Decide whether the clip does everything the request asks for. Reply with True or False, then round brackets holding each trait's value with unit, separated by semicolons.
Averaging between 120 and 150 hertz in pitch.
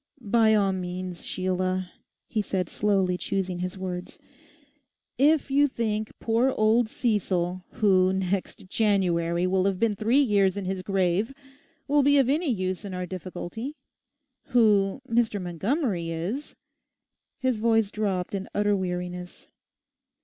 False (195 Hz)